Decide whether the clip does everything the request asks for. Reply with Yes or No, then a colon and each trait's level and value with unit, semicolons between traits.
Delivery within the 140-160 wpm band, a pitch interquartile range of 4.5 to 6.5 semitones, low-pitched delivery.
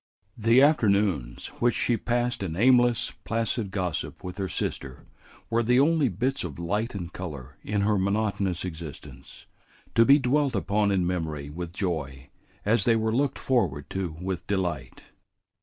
Yes: average, 155 wpm; wide, 5.4 semitones; low, 100 Hz